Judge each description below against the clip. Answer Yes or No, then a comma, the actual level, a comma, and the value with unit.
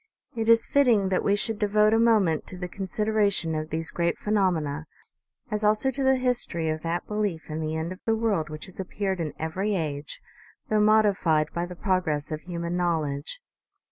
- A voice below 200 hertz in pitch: Yes, medium, 185 Hz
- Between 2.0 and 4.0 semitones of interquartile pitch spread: No, average, 4.9 semitones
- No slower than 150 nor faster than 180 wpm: No, average, 195 wpm